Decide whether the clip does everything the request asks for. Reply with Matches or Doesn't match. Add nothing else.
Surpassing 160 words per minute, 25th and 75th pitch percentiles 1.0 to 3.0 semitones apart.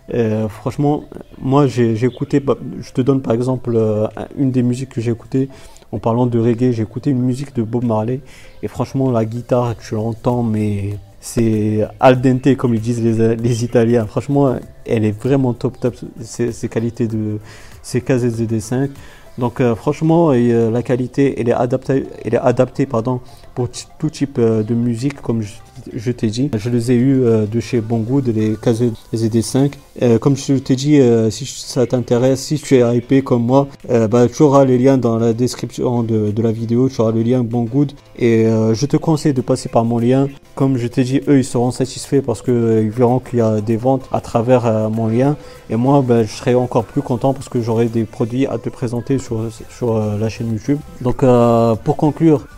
Matches